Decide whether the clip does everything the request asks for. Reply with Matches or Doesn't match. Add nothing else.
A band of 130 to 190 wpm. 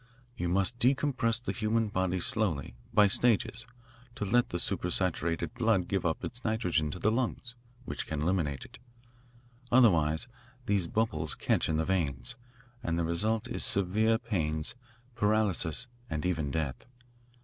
Matches